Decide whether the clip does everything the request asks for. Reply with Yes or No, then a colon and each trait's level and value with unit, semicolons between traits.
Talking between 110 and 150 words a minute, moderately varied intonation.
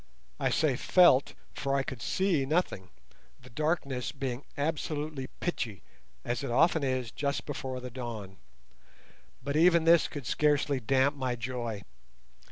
Yes: average, 140 wpm; average, 3.4 semitones